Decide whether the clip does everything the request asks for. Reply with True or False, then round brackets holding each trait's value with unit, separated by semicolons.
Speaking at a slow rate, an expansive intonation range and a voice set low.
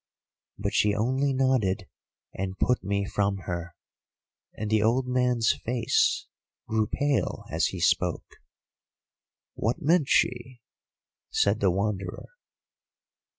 False (110 wpm; 4.1 semitones; 110 Hz)